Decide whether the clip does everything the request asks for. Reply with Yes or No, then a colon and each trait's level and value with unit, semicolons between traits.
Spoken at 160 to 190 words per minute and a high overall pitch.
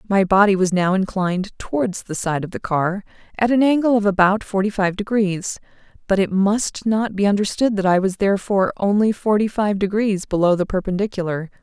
Yes: average, 185 wpm; high, 200 Hz